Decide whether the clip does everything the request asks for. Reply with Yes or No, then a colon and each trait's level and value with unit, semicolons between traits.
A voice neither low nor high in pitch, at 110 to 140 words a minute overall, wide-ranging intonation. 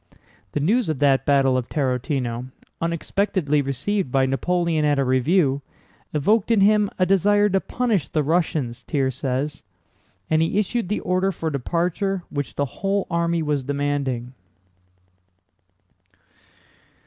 Yes: medium, 155 Hz; slow, 135 wpm; wide, 5.8 semitones